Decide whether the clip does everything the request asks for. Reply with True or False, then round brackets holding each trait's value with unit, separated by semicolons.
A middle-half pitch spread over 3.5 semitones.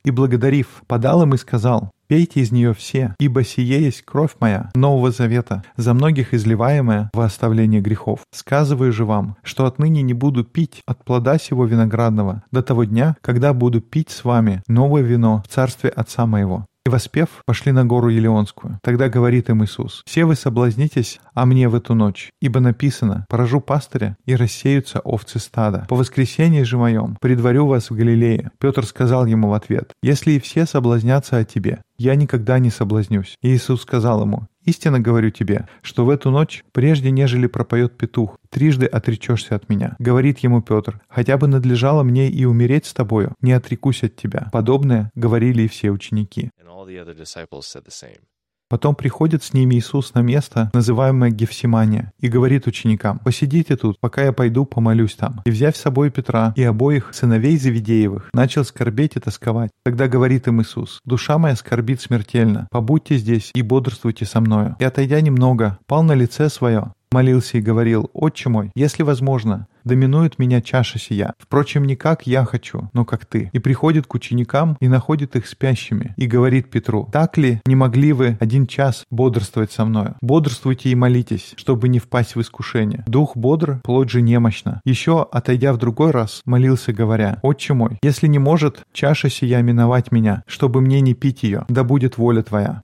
False (3.0 semitones)